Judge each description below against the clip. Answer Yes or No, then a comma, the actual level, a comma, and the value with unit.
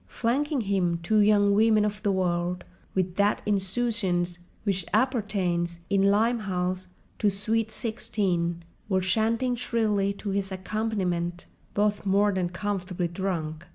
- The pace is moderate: No, slow, 120 wpm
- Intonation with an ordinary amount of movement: Yes, average, 3.1 semitones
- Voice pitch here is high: Yes, high, 200 Hz